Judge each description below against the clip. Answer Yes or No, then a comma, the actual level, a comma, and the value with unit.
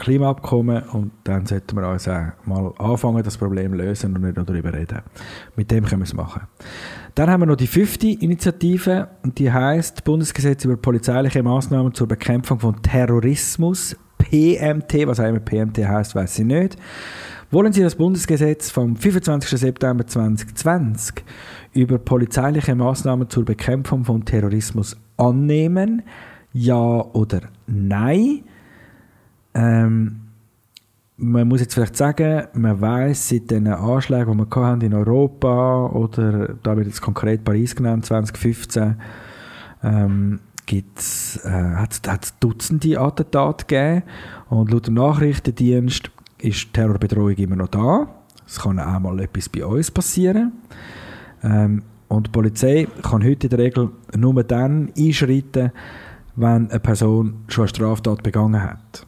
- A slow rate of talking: No, average, 135 wpm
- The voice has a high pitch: No, low, 115 Hz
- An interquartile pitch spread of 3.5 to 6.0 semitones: Yes, average, 3.8 semitones